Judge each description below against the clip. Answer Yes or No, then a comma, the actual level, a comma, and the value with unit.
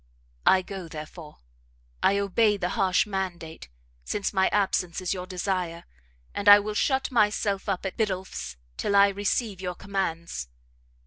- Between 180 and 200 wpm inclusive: No, average, 145 wpm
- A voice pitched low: No, high, 190 Hz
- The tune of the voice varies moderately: No, narrow, 2.2 semitones